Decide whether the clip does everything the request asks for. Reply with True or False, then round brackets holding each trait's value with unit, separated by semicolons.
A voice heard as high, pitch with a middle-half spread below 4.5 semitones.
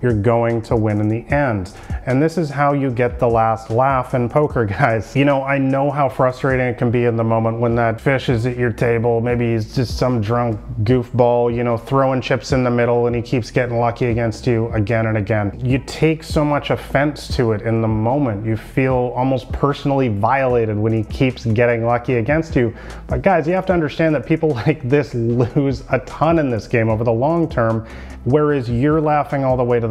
False (125 Hz; 3.1 semitones)